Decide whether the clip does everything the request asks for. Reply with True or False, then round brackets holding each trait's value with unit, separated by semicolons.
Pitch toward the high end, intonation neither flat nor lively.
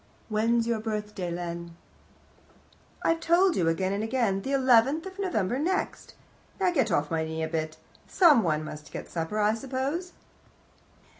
False (220 Hz; 8.2 semitones)